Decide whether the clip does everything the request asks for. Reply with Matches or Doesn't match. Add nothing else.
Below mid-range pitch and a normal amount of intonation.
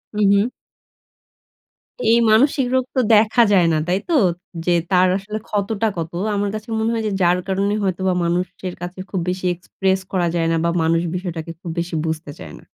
Doesn't match